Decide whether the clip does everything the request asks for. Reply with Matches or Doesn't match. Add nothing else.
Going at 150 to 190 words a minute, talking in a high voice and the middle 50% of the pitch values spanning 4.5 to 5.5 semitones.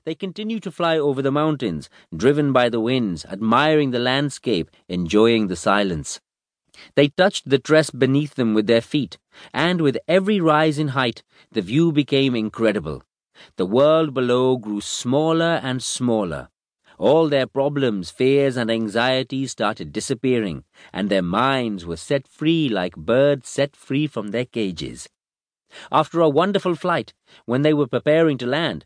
Doesn't match